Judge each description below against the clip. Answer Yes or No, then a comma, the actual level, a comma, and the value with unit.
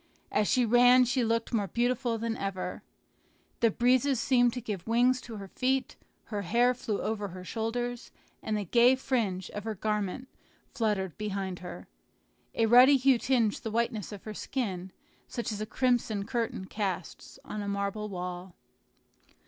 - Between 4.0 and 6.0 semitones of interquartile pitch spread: No, average, 3.5 semitones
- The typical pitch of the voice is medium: No, high, 225 Hz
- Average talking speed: Yes, average, 165 wpm